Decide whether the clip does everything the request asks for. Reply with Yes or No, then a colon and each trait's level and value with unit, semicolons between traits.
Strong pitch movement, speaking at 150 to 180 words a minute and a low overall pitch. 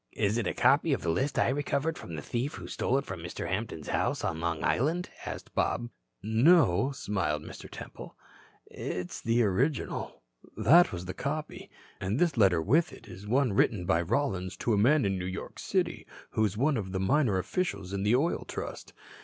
No: wide, 7.0 semitones; average, 200 wpm; low, 110 Hz